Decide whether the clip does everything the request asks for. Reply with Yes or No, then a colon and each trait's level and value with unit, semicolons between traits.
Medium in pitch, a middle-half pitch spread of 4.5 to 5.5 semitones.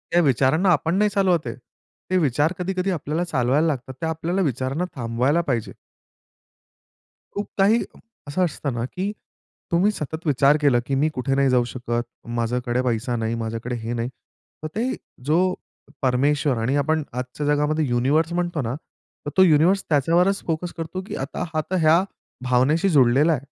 Yes: medium, 145 Hz; average, 5.2 semitones